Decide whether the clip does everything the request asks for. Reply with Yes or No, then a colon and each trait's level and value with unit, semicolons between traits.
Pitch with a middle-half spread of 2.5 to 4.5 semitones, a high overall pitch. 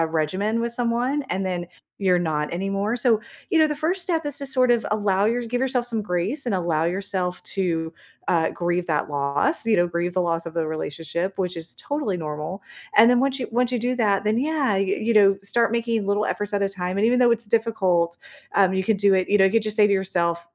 No: average, 5.0 semitones; high, 200 Hz